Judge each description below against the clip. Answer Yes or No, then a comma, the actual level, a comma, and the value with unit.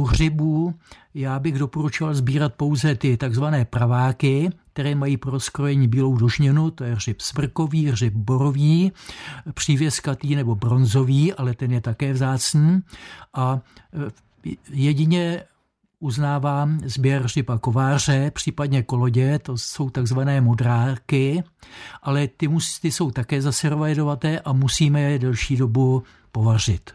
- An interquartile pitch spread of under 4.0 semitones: Yes, average, 2.7 semitones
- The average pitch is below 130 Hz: No, medium, 140 Hz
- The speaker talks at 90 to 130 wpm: Yes, average, 120 wpm